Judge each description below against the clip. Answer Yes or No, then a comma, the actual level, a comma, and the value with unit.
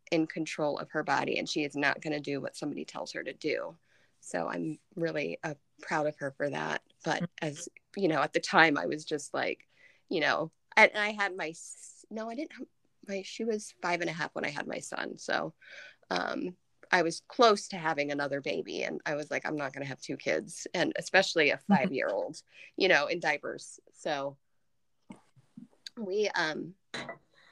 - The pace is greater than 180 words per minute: Yes, fast, 205 wpm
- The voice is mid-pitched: Yes, medium, 165 Hz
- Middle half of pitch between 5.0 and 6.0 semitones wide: Yes, wide, 5.4 semitones